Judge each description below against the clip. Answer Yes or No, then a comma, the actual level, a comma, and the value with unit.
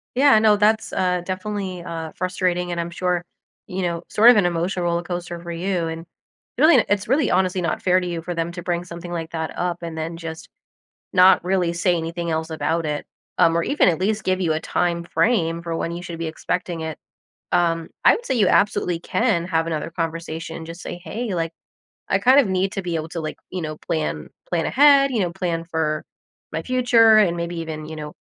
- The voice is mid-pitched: Yes, medium, 175 Hz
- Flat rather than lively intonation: Yes, narrow, 2.3 semitones